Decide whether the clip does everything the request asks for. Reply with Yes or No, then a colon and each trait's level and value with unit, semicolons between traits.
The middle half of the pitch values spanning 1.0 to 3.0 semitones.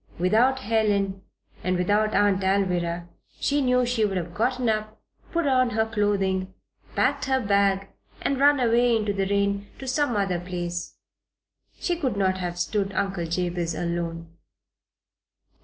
No: average, 4.6 semitones